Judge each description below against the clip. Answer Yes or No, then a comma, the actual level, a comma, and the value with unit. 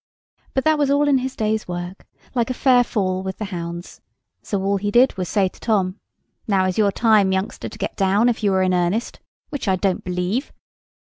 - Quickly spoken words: Yes, fast, 220 wpm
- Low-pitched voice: No, high, 200 Hz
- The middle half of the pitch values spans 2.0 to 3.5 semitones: No, average, 4.3 semitones